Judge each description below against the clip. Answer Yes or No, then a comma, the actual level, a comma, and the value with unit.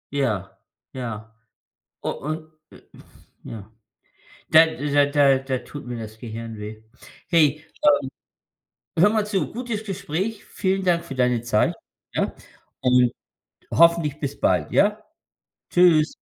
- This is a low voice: No, medium, 145 Hz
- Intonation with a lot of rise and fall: Yes, wide, 5.8 semitones